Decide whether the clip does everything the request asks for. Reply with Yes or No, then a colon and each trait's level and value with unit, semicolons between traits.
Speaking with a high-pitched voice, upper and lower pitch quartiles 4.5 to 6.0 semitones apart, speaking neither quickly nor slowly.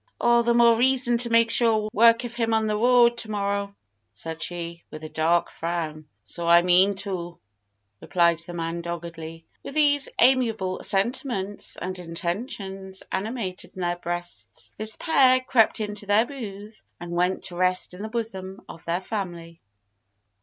Yes: high, 195 Hz; average, 5.0 semitones; average, 160 wpm